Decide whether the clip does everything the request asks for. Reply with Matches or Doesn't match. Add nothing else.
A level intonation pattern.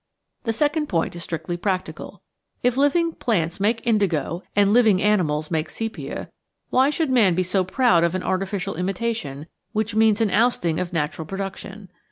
Doesn't match